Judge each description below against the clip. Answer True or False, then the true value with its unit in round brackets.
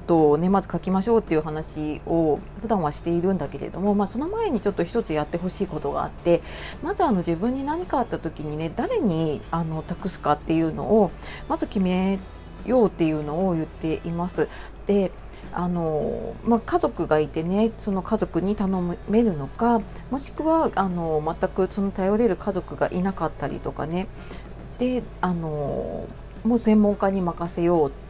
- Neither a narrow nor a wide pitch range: True (4.6 semitones)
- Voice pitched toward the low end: False (185 Hz)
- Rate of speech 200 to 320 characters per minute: False (345 characters per minute)